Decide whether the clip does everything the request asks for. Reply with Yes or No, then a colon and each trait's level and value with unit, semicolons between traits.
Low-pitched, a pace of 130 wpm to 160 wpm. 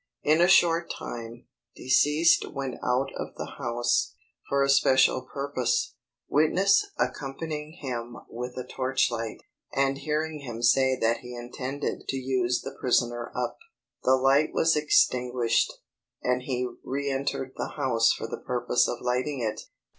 Yes: low, 130 Hz; average, 140 wpm